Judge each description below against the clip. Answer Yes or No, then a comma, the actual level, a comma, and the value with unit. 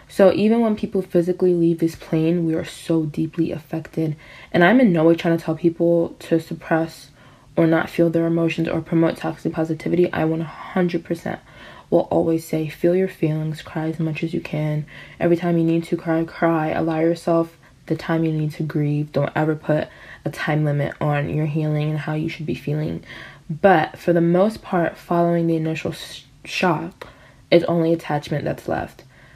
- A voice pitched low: No, medium, 165 Hz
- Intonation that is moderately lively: No, narrow, 1.6 semitones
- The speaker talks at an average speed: Yes, average, 185 wpm